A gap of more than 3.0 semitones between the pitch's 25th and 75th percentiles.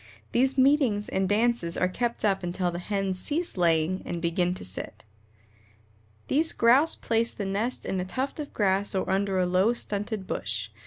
Yes: average, 4.6 semitones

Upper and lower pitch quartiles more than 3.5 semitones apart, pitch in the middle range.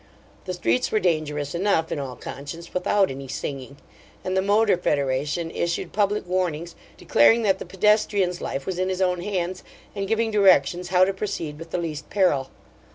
Yes: average, 4.6 semitones; medium, 180 Hz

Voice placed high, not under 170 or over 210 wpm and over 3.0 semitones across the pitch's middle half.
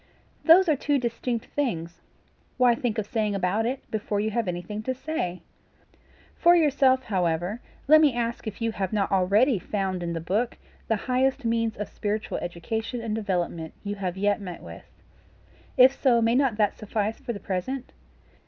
Yes: high, 220 Hz; average, 175 wpm; average, 4.4 semitones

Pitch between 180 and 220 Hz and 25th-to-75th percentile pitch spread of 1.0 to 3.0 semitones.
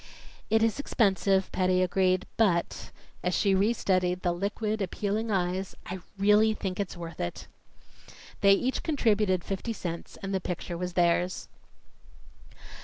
Yes: high, 190 Hz; narrow, 2.6 semitones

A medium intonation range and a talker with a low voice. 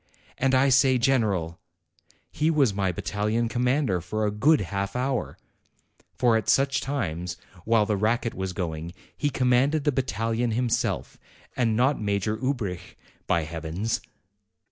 Yes: average, 4.9 semitones; low, 115 Hz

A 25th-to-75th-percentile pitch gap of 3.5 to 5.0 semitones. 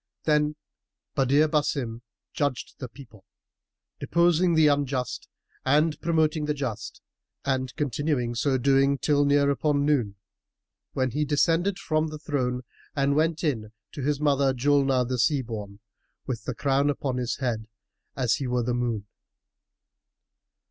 No: average, 3.1 semitones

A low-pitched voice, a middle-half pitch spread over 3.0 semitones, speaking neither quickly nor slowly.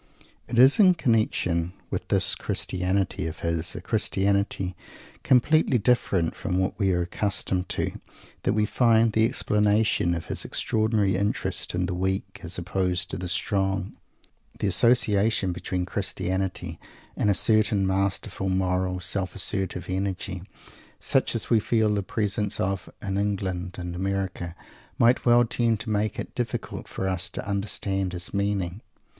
No: very low, 95 Hz; narrow, 2.5 semitones; average, 150 wpm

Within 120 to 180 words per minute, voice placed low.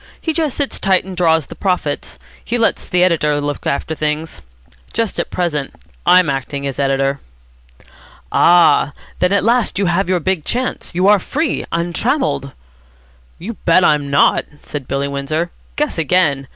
No: average, 160 wpm; medium, 170 Hz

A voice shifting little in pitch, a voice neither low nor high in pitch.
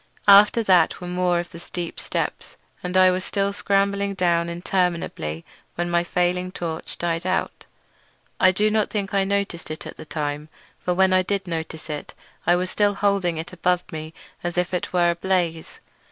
Yes: narrow, 2.2 semitones; medium, 180 Hz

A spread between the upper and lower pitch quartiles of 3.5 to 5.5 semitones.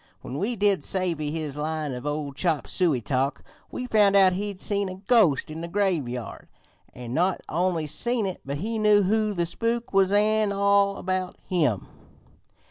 Yes: average, 5.1 semitones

